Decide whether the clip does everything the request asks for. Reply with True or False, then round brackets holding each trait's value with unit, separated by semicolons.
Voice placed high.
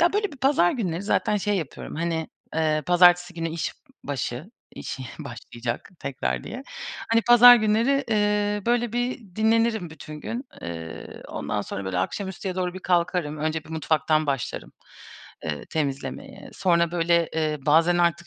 False (175 Hz)